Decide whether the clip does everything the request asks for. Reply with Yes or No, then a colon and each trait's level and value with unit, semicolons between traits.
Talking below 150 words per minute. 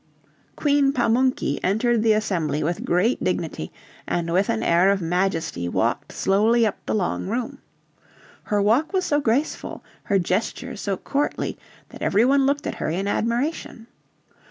No: average, 155 wpm